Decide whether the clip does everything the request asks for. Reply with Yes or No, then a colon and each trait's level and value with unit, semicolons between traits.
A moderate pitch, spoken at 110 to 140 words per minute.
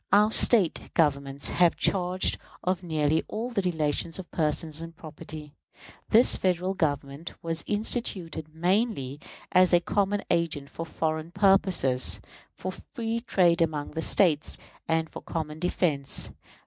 Yes: medium, 170 Hz; slow, 135 wpm